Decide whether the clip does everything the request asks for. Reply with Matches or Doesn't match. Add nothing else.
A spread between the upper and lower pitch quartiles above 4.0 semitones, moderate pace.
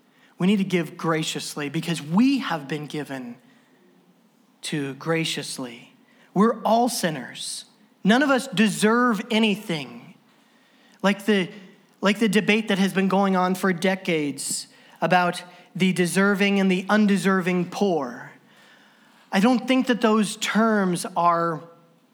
Doesn't match